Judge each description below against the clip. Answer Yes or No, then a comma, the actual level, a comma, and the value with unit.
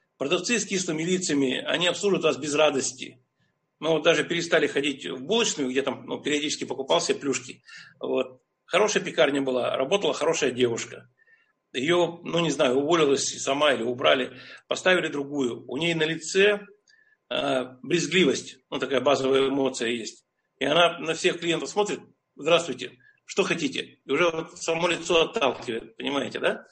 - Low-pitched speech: No, medium, 160 Hz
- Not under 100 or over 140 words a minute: No, average, 150 wpm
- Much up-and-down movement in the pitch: No, average, 4.5 semitones